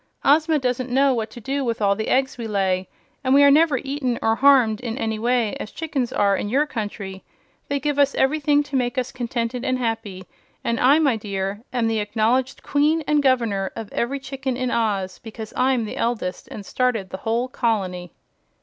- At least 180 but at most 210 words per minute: Yes, average, 200 wpm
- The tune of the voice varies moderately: Yes, average, 3.9 semitones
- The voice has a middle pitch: No, high, 245 Hz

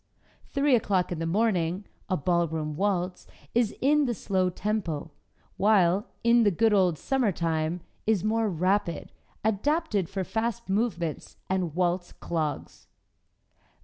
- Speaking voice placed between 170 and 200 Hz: Yes, high, 190 Hz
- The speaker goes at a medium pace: No, slow, 125 wpm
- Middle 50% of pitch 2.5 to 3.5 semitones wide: No, average, 4.4 semitones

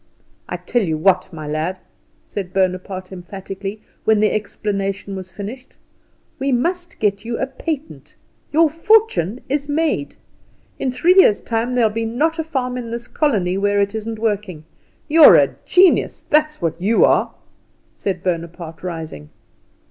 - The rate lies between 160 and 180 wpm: No, average, 150 wpm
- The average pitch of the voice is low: No, high, 210 Hz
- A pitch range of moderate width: No, wide, 6.3 semitones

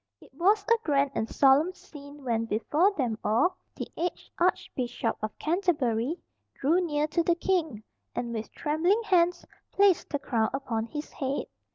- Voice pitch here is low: No, very high, 295 Hz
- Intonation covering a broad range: Yes, wide, 6.6 semitones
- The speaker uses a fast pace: No, average, 160 wpm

